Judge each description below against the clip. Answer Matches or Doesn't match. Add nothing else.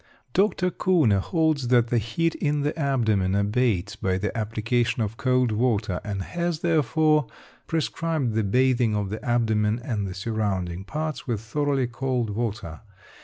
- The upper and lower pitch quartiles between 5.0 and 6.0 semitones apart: Matches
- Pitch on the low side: Matches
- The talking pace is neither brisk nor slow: Matches